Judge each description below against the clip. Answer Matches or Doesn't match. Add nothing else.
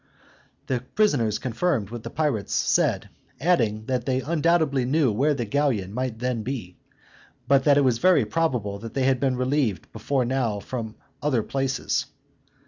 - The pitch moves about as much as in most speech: Matches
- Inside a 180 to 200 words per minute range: Doesn't match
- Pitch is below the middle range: Matches